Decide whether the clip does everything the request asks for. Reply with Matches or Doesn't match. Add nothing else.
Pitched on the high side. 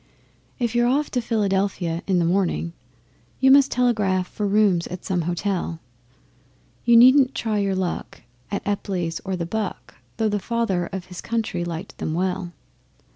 Matches